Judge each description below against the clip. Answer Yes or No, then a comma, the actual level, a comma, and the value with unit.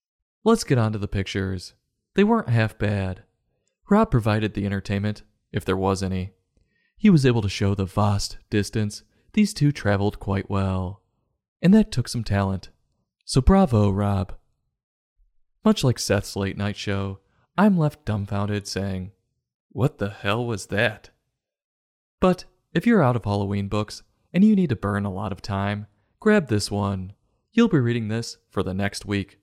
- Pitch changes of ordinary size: Yes, average, 3.6 semitones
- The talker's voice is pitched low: Yes, low, 105 Hz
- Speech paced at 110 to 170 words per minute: Yes, average, 165 wpm